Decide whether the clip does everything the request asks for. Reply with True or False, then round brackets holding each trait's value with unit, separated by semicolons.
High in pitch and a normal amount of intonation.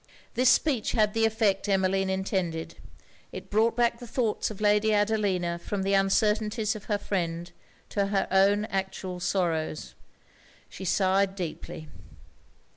False (200 Hz; 2.2 semitones)